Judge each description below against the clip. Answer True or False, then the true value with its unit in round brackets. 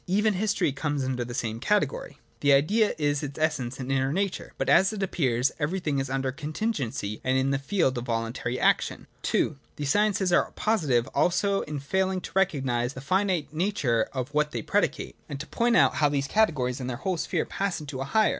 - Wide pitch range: True (6.4 semitones)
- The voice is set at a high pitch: False (145 Hz)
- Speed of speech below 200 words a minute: False (205 wpm)